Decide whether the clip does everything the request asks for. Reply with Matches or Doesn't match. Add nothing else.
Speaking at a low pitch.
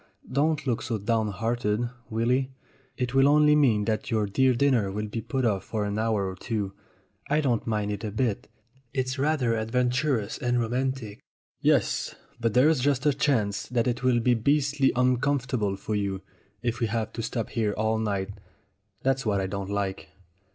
Matches